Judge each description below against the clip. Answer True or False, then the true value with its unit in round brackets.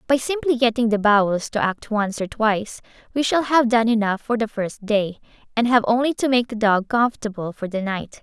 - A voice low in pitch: False (225 Hz)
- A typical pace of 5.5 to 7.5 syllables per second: False (5.3 syllables/s)